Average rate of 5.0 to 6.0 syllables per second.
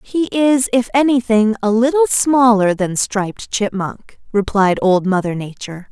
No: 4.4 syllables/s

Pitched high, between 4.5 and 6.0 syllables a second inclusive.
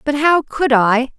No: very high, 270 Hz; 3.8 syllables/s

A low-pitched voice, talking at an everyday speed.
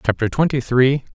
Yes: low, 130 Hz; average, 155 wpm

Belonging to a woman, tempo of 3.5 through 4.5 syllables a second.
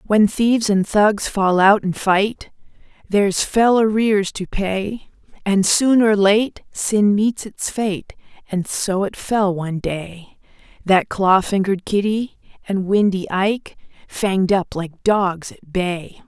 Yes: female; 3.7 syllables/s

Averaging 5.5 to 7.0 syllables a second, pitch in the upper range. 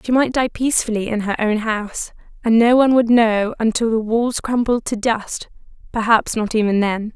No: 5.1 syllables/s; high, 225 Hz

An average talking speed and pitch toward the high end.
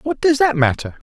No: fast, 215 wpm; high, 195 Hz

